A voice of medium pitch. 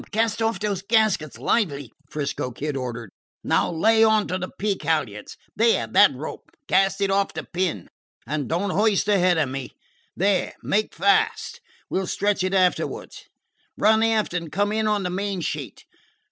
No: high, 195 Hz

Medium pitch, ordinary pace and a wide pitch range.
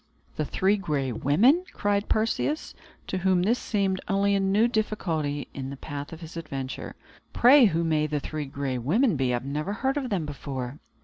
Yes: medium, 165 Hz; average, 185 wpm; wide, 6.4 semitones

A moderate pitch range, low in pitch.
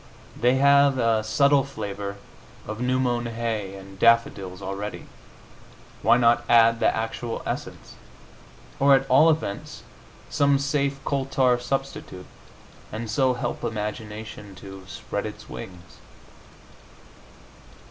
Yes: average, 4.2 semitones; low, 115 Hz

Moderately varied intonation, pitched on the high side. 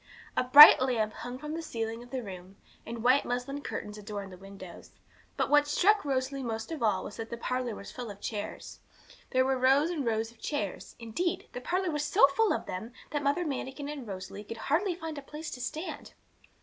Yes: average, 4.9 semitones; very high, 255 Hz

